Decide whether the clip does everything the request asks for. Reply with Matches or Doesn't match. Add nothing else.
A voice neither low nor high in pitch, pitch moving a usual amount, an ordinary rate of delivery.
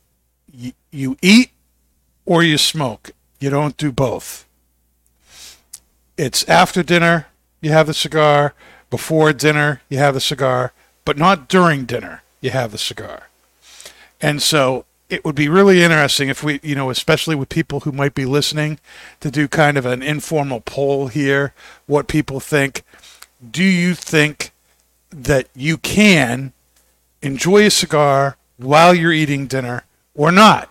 Matches